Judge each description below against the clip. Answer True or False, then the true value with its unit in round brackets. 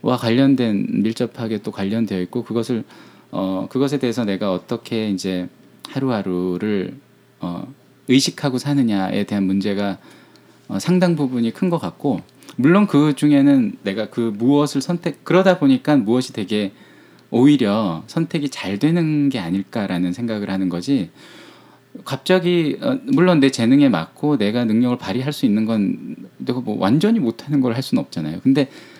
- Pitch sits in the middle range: False (125 Hz)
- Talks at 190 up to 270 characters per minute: False (310 characters per minute)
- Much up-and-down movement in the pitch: True (6.2 semitones)